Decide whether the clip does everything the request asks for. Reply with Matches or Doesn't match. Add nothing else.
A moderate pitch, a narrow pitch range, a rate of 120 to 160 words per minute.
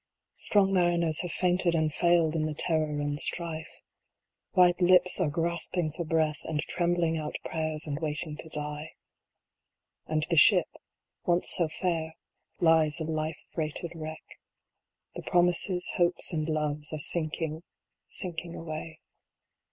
Matches